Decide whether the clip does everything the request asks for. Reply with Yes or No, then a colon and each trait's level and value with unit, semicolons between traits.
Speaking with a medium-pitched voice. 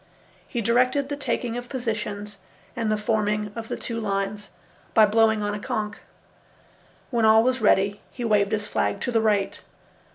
No: high, 215 Hz